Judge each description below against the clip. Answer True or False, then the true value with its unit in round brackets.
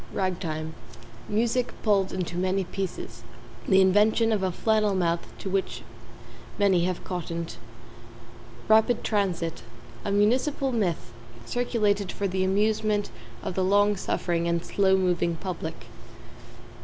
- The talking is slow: True (125 wpm)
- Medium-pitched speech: False (195 Hz)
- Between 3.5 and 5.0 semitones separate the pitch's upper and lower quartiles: False (2.8 semitones)